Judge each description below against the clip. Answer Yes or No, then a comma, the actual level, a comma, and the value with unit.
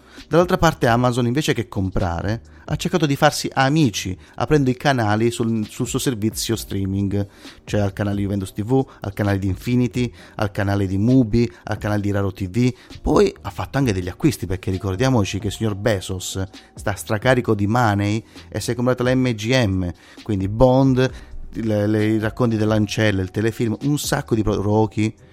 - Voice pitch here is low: Yes, low, 110 Hz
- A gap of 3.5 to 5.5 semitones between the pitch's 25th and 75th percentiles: Yes, average, 3.8 semitones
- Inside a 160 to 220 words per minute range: Yes, average, 165 wpm